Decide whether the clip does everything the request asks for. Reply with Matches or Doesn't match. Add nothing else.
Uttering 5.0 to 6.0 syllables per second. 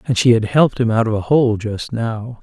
Matches